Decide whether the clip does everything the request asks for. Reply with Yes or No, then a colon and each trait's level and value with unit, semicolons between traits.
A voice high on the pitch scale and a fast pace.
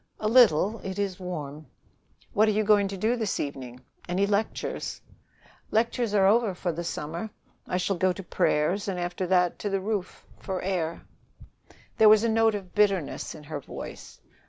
No: high, 195 Hz; average, 180 wpm